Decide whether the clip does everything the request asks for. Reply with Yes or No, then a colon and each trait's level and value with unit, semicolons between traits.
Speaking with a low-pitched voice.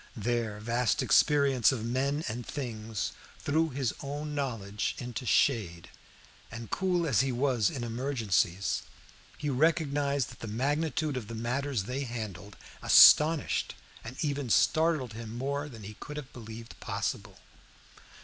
Yes: low, 125 Hz